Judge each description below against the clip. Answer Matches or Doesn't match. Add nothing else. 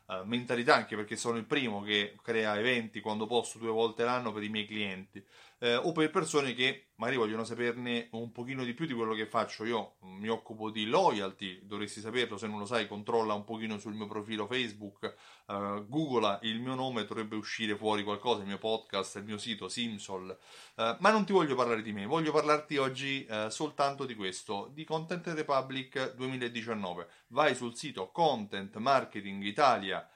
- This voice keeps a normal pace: Doesn't match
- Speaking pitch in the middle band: Doesn't match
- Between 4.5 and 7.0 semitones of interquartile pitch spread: Doesn't match